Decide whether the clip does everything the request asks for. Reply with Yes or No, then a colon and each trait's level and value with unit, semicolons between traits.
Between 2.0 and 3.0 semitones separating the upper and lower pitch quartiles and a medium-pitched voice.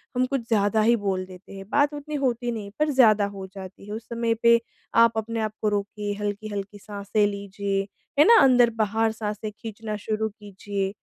No: narrow, 2.5 semitones; high, 215 Hz